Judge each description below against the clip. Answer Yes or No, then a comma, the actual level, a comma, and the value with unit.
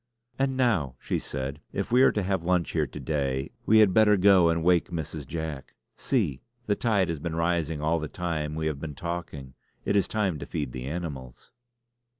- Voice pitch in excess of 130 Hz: No, very low, 85 Hz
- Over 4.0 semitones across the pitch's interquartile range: Yes, average, 4.4 semitones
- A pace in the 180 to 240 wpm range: Yes, average, 200 wpm